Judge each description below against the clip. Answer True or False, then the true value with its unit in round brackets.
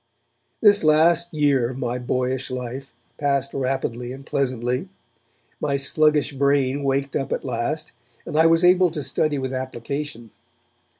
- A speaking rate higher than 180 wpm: False (140 wpm)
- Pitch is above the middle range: False (140 Hz)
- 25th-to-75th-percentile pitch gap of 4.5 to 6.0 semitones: False (2.9 semitones)